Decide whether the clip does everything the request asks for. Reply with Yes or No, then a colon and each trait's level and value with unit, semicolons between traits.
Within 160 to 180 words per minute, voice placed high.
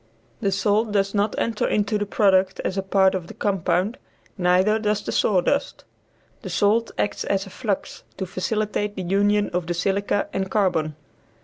Yes: average, 175 wpm; high, 200 Hz